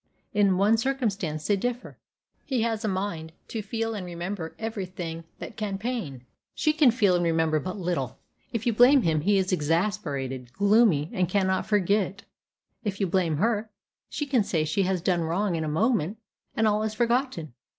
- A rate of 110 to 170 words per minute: No, average, 185 wpm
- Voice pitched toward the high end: Yes, high, 195 Hz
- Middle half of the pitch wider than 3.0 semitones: Yes, average, 4.9 semitones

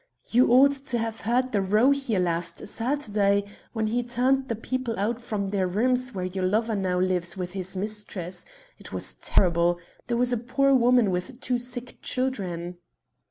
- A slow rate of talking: No, average, 175 wpm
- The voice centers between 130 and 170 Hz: No, high, 220 Hz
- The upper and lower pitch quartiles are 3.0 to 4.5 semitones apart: No, average, 5.0 semitones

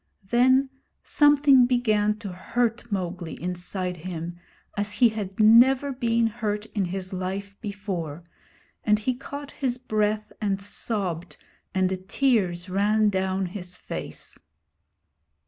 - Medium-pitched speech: No, high, 205 Hz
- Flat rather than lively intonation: No, average, 4.1 semitones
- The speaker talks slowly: Yes, slow, 125 wpm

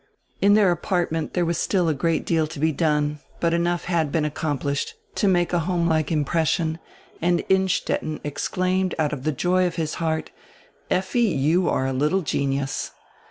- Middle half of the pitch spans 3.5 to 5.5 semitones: No, average, 2.8 semitones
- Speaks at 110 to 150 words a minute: No, average, 170 wpm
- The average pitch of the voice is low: No, medium, 165 Hz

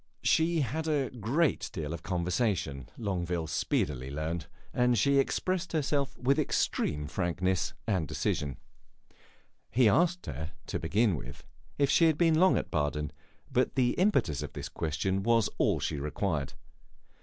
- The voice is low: Yes, low, 100 Hz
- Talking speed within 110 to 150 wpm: Yes, average, 145 wpm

